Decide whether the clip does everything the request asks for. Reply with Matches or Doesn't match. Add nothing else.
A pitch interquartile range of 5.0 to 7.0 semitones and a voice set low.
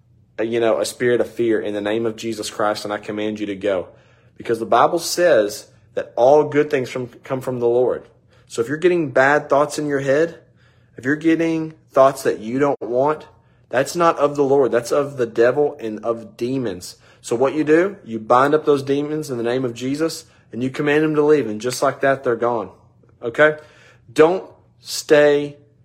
Doesn't match